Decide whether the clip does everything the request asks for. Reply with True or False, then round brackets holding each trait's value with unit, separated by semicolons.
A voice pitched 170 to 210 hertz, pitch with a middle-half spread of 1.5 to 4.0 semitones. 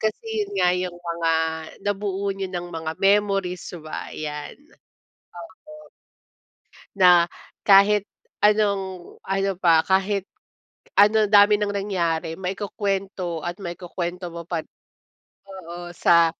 True (190 Hz; 2.7 semitones)